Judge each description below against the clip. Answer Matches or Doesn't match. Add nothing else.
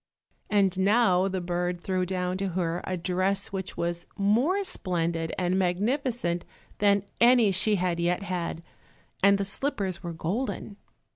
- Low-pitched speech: Doesn't match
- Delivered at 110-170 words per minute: Matches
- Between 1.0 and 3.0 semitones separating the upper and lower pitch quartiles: Matches